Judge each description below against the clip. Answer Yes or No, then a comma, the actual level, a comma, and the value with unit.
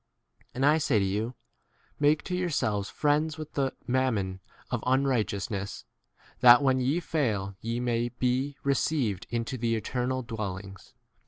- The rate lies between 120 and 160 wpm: Yes, average, 155 wpm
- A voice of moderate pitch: No, low, 125 Hz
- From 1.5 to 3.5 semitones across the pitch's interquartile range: No, average, 4.5 semitones